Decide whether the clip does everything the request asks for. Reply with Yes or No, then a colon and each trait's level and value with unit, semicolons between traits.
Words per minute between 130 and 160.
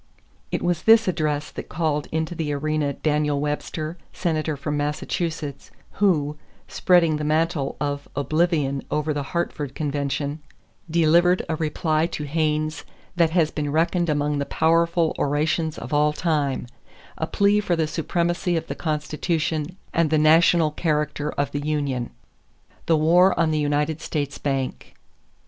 Yes: average, 145 wpm